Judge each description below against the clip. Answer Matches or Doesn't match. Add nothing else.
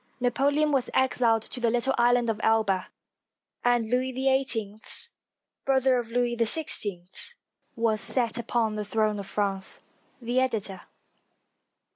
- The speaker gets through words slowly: Matches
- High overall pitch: Matches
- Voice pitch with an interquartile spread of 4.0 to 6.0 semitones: Doesn't match